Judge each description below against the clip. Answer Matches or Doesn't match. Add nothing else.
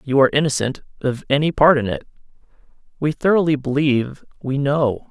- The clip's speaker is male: Matches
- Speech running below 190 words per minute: Matches